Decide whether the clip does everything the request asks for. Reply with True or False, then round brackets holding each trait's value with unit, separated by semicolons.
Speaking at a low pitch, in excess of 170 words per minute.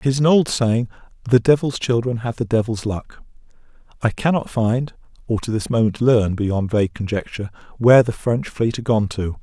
True (115 Hz; 180 wpm)